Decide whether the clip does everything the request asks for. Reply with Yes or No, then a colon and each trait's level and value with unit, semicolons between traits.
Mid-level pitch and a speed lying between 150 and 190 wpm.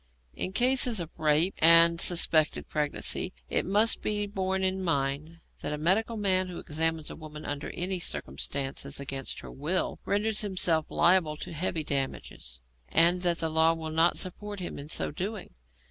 Yes: medium, 170 Hz; average, 165 wpm